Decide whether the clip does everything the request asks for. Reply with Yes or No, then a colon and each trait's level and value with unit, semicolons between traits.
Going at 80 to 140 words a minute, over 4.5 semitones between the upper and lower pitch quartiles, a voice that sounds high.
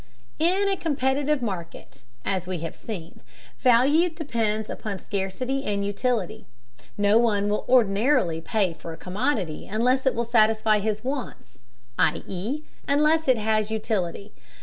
Yes: slow, 135 wpm; average, 5.0 semitones; high, 220 Hz